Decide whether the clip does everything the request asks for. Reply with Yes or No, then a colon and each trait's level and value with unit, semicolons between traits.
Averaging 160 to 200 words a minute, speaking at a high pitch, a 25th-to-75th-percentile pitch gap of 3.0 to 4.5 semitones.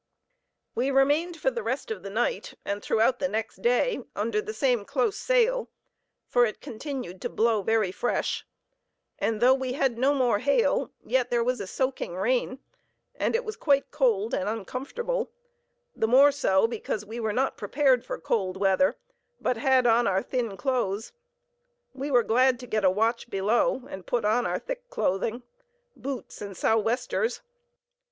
Yes: average, 170 wpm; high, 240 Hz; average, 3.9 semitones